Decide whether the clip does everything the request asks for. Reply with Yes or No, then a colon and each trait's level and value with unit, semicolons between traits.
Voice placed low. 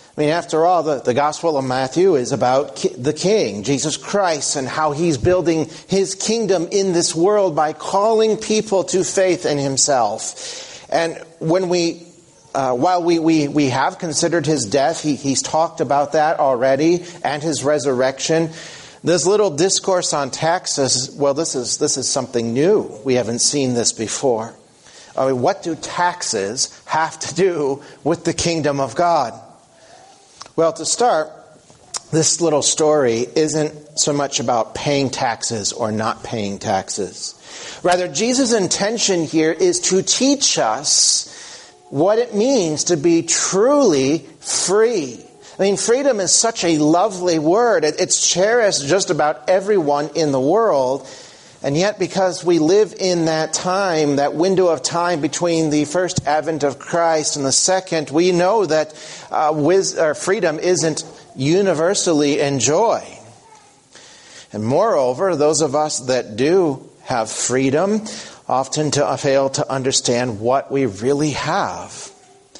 No: medium, 160 Hz